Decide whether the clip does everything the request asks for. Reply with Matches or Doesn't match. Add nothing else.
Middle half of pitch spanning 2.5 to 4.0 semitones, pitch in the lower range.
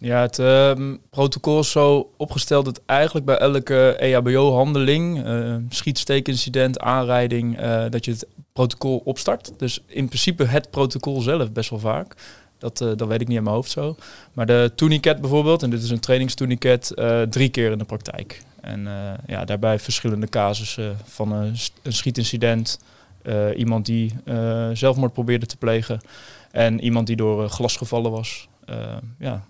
Matches